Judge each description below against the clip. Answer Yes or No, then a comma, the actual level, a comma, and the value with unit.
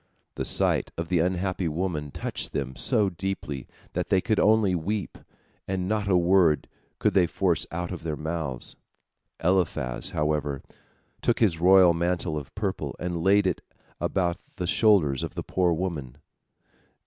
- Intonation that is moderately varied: Yes, average, 3.5 semitones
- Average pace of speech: Yes, average, 155 wpm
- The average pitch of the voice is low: Yes, very low, 90 Hz